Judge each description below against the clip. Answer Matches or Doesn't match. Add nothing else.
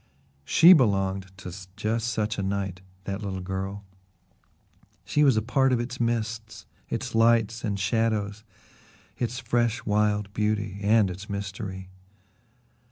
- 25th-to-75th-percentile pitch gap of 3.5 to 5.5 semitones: Doesn't match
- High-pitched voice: Doesn't match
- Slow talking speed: Matches